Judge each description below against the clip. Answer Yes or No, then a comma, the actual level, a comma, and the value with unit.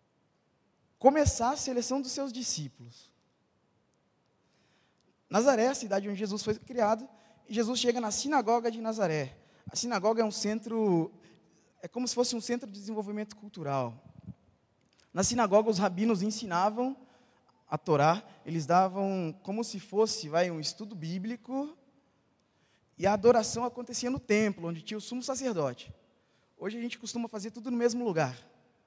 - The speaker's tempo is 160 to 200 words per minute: No, average, 150 wpm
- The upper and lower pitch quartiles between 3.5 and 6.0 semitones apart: Yes, average, 4.5 semitones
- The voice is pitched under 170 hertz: No, high, 215 Hz